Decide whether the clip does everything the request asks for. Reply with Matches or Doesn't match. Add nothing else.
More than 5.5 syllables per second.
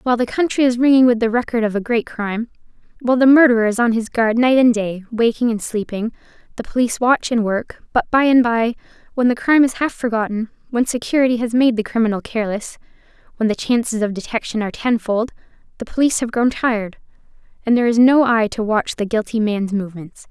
Matches